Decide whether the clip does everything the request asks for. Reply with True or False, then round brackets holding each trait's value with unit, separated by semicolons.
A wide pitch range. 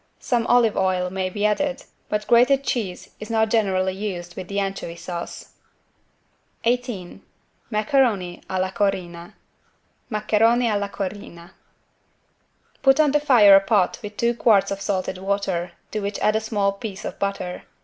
False (3.3 semitones)